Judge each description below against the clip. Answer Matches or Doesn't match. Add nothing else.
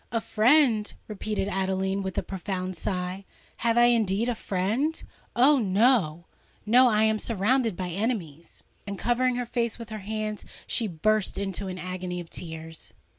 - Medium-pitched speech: Doesn't match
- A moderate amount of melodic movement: Matches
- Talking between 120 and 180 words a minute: Matches